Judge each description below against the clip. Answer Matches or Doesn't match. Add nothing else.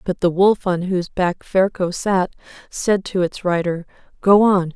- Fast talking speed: Doesn't match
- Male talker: Doesn't match